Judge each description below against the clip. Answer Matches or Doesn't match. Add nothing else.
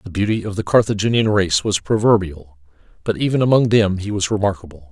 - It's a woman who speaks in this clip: Doesn't match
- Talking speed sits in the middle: Matches